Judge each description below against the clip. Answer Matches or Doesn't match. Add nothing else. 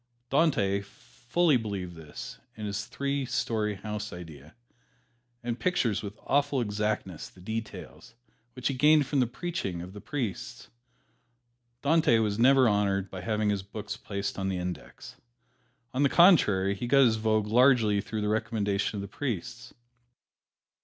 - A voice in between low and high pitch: Doesn't match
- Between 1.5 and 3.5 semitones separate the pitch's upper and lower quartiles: Doesn't match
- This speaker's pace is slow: Doesn't match